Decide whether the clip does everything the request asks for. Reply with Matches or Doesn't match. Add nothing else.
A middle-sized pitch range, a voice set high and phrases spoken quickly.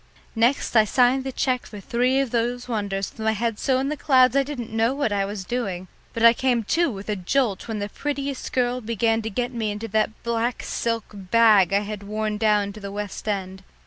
Matches